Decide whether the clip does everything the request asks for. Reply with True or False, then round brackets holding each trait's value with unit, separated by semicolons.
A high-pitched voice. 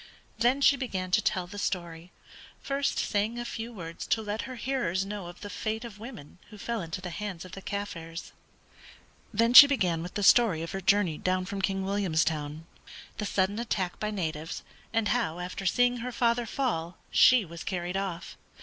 True (195 Hz)